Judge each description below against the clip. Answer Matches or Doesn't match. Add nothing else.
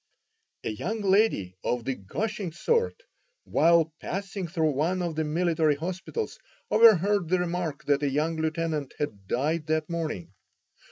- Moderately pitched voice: Matches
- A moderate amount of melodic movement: Matches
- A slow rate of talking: Doesn't match